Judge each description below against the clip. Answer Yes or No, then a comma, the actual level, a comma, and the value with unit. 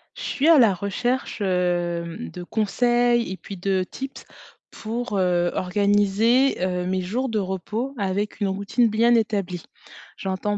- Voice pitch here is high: Yes, high, 200 Hz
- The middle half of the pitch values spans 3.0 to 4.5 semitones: Yes, average, 4.1 semitones